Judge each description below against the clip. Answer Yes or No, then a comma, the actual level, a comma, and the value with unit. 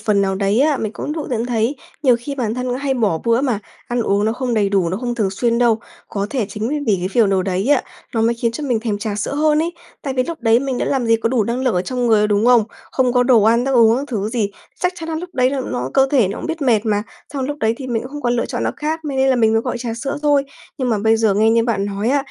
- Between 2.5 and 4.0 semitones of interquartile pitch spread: Yes, average, 3.7 semitones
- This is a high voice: Yes, high, 235 Hz